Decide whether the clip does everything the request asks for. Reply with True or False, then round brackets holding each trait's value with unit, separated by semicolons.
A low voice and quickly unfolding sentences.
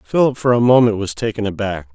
True (110 Hz; 215 wpm)